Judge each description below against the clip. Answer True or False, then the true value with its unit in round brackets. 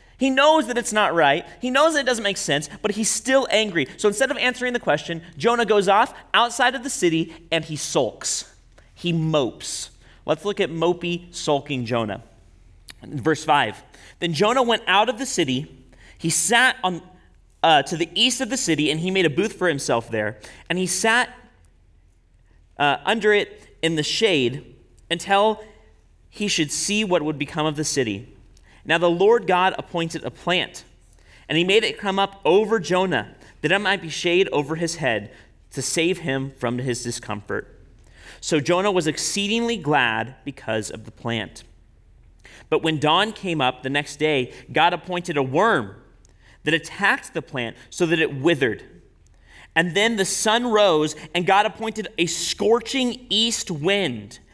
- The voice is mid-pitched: True (170 Hz)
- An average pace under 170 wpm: False (175 wpm)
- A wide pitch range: True (7.6 semitones)